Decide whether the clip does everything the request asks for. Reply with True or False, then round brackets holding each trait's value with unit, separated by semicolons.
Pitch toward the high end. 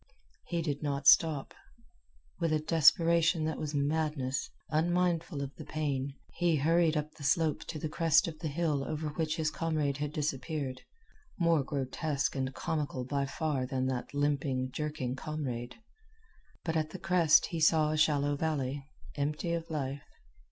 False (150 Hz)